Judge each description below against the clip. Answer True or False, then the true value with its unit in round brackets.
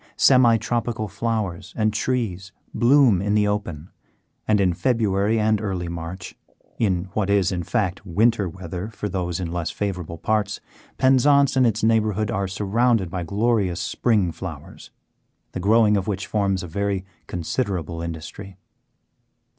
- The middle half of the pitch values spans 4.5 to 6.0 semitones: False (3.5 semitones)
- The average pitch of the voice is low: True (100 Hz)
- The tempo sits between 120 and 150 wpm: True (145 wpm)